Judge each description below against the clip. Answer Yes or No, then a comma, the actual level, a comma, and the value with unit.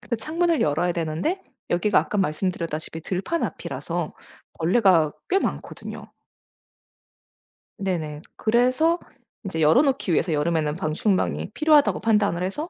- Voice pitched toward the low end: No, medium, 185 Hz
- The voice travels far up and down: Yes, wide, 7.8 semitones